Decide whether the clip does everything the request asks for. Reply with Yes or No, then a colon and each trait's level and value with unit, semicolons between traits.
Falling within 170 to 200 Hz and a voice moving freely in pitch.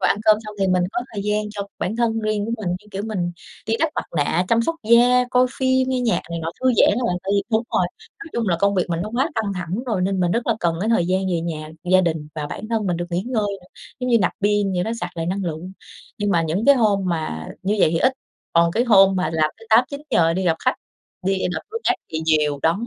No: high, 195 Hz; average, 4.7 semitones